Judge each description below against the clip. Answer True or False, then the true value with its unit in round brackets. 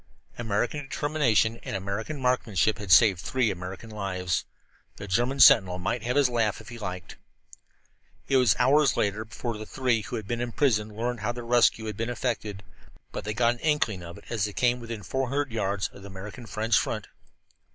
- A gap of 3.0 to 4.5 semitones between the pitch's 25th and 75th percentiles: True (3.4 semitones)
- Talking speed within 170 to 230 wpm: True (195 wpm)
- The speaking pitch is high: False (115 Hz)